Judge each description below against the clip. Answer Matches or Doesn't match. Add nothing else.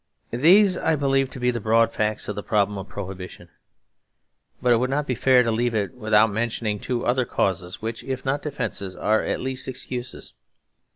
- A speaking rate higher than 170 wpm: Matches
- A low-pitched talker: Matches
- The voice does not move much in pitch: Doesn't match